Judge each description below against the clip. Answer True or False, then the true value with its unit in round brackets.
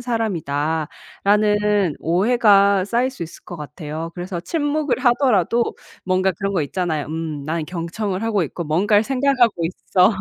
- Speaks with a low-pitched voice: False (190 Hz)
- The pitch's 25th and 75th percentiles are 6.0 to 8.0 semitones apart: False (5.3 semitones)